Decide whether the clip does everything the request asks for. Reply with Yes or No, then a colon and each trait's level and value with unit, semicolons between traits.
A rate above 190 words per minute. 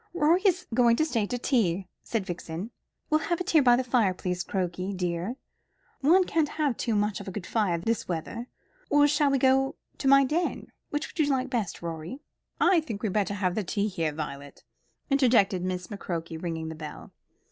Yes: average, 200 wpm